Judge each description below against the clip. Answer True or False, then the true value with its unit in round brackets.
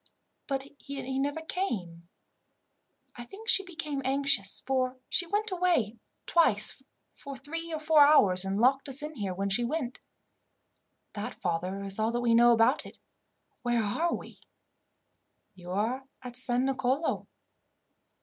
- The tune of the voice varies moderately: False (5.8 semitones)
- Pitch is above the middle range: True (260 Hz)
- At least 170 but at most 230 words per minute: False (140 wpm)